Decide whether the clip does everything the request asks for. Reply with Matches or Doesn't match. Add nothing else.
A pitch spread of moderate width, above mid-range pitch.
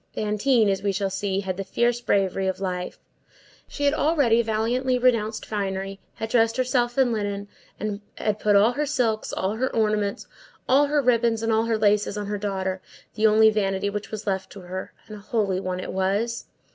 Matches